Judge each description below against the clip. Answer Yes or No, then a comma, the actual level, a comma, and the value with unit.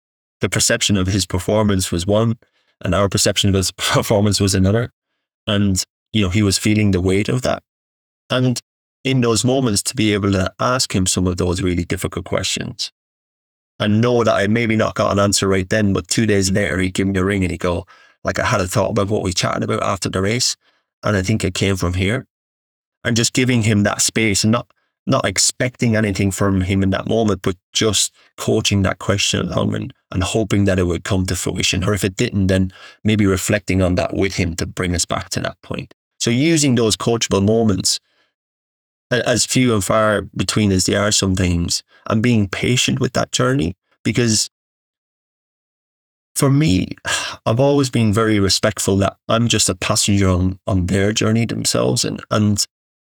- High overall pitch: No, low, 100 Hz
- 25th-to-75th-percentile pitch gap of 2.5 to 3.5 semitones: Yes, average, 2.8 semitones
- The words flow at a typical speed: Yes, average, 195 wpm